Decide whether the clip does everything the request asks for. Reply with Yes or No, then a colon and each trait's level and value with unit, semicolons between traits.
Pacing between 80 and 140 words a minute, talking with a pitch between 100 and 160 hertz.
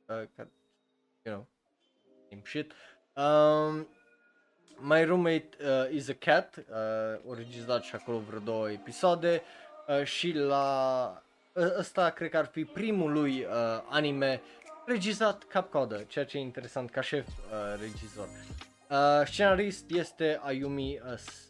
Yes: average, 130 wpm; medium, 140 Hz